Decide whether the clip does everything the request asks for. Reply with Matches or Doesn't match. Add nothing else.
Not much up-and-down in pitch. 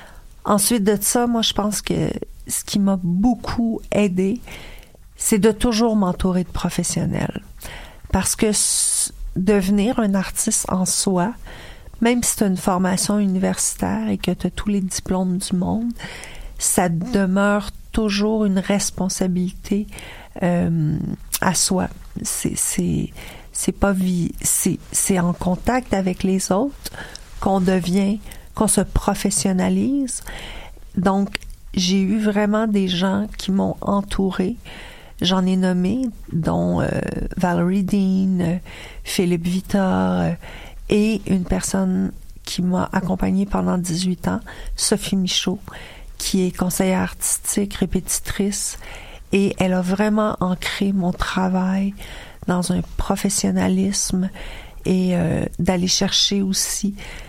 Matches